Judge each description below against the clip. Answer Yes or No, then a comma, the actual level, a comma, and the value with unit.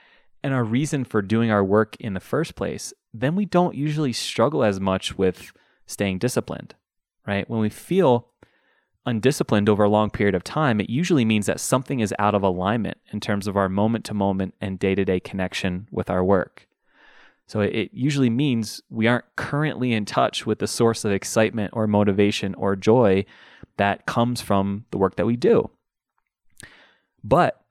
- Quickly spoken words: No, average, 180 wpm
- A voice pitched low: Yes, low, 105 Hz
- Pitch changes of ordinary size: Yes, average, 3.5 semitones